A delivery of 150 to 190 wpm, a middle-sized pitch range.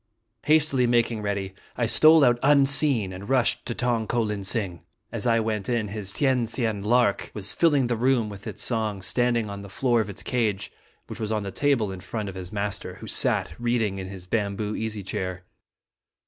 No: average, 200 wpm; average, 3.4 semitones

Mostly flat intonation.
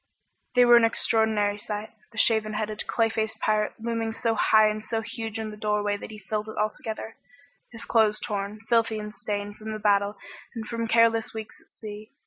Yes: narrow, 1.2 semitones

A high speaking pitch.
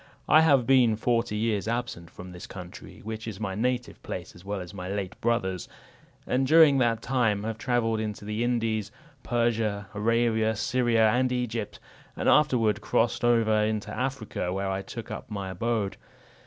No: low, 110 Hz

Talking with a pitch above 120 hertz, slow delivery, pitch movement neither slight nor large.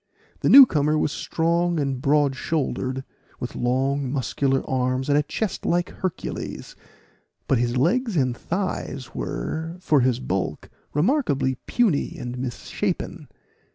Yes: medium, 140 Hz; slow, 130 wpm; average, 4.6 semitones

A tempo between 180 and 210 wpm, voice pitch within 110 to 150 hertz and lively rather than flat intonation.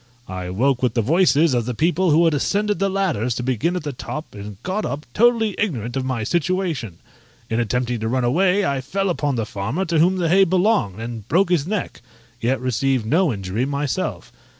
Yes: fast, 205 wpm; medium, 140 Hz; wide, 7.2 semitones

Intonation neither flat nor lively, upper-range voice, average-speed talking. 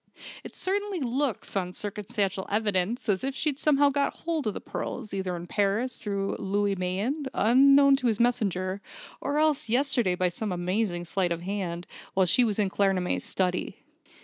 No: wide, 5.9 semitones; high, 205 Hz; average, 170 wpm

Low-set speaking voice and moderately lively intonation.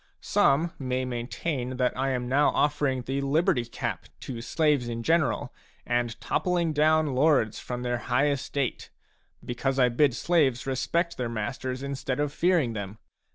Yes: low, 130 Hz; average, 3.2 semitones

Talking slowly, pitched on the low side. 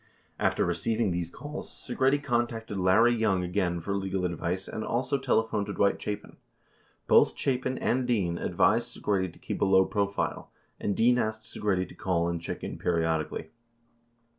No: average, 160 wpm; low, 100 Hz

